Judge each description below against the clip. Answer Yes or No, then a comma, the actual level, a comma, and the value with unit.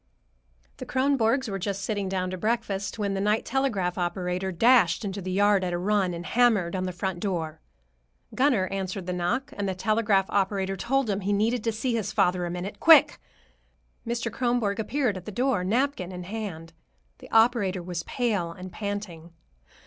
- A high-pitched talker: Yes, high, 200 Hz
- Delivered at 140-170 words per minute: No, average, 180 wpm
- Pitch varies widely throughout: No, average, 3.7 semitones